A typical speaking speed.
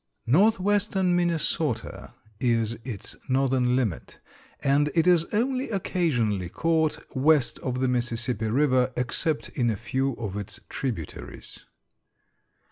No: slow, 115 wpm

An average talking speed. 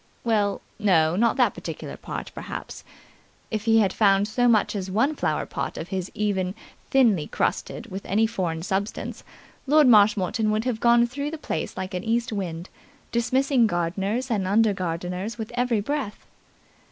Yes: average, 165 wpm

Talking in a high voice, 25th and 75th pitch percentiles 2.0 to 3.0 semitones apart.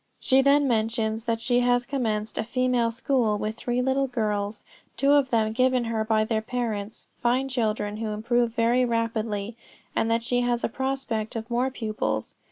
Yes: high, 230 Hz; narrow, 2.5 semitones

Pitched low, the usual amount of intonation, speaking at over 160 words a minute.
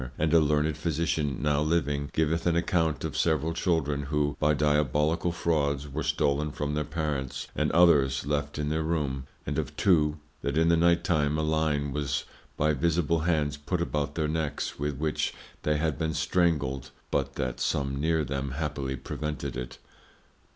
No: very low, 75 Hz; narrow, 2.0 semitones; average, 170 wpm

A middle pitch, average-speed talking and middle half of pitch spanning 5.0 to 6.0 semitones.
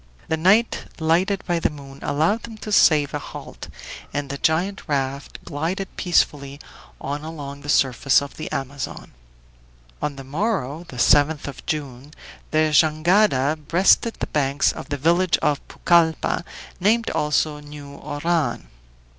No: medium, 150 Hz; average, 145 wpm; average, 3.5 semitones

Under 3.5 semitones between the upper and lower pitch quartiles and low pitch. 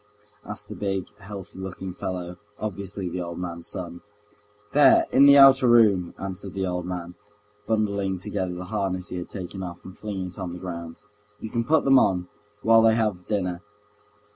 Yes: average, 2.8 semitones; very low, 95 Hz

